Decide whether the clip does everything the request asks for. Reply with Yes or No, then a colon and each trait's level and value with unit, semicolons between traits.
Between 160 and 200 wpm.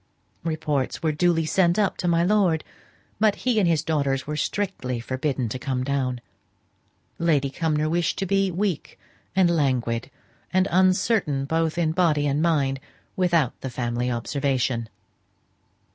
No: average, 140 wpm